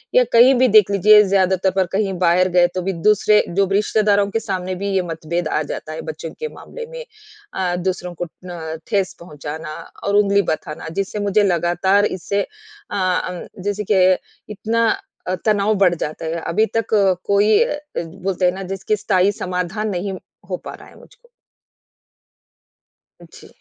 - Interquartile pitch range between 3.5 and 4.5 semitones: No, average, 2.8 semitones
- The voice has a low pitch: No, high, 190 Hz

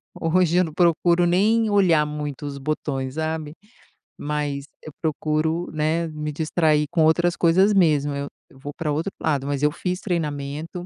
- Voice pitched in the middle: Yes, medium, 155 Hz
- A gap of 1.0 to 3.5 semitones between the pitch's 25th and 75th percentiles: Yes, average, 2.7 semitones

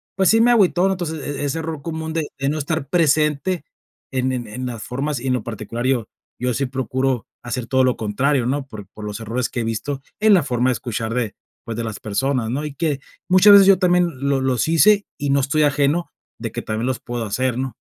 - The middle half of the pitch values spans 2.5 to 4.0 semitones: No, average, 4.6 semitones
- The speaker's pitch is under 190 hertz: Yes, low, 135 Hz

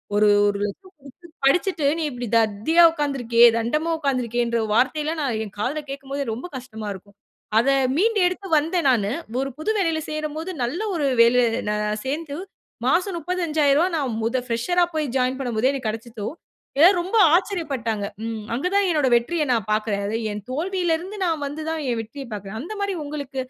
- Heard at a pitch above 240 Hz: Yes, very high, 275 Hz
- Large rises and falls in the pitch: Yes, wide, 5.9 semitones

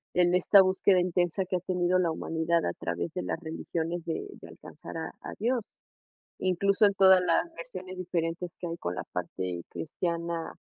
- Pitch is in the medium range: Yes, medium, 175 Hz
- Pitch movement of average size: No, narrow, 2.3 semitones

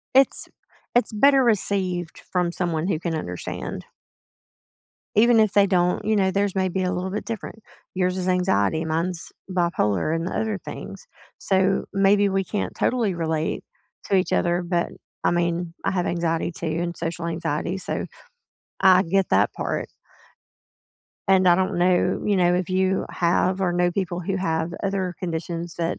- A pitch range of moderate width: No, narrow, 2.2 semitones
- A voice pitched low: No, medium, 180 Hz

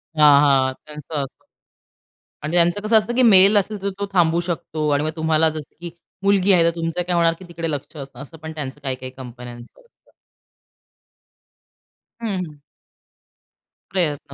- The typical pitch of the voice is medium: Yes, medium, 160 Hz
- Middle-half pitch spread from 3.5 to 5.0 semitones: Yes, average, 3.9 semitones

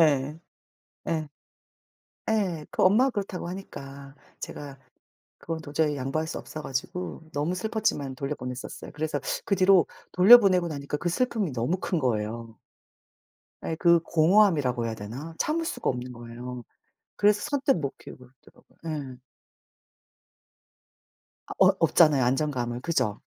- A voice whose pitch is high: No, medium, 155 Hz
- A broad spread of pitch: Yes, wide, 5.7 semitones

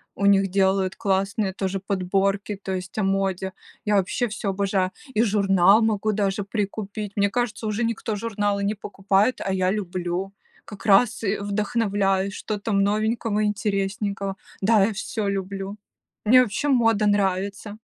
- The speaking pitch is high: Yes, high, 200 Hz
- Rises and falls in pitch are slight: Yes, narrow, 1.6 semitones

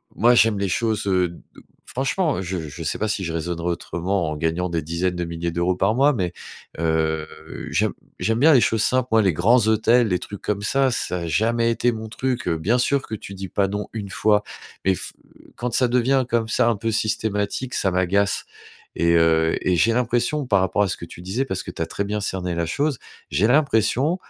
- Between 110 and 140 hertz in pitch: No, low, 100 Hz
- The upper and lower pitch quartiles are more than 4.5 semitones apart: Yes, average, 5.2 semitones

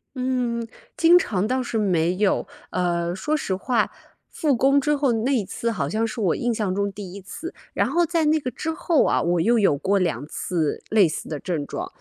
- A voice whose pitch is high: Yes, high, 220 Hz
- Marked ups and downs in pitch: Yes, wide, 6.1 semitones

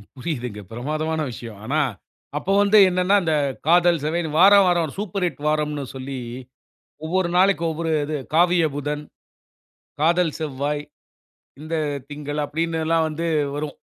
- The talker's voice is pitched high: No, medium, 160 Hz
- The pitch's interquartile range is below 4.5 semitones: Yes, average, 2.9 semitones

